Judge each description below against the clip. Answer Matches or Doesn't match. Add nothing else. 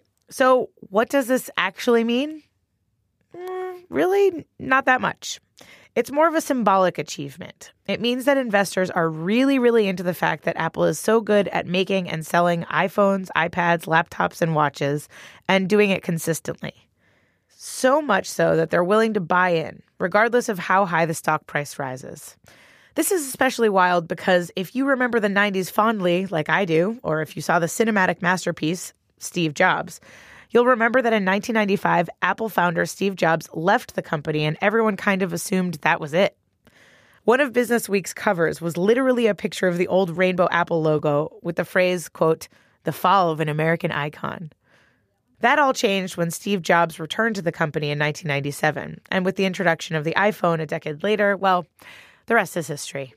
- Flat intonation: Doesn't match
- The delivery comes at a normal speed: Matches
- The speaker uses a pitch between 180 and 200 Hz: Matches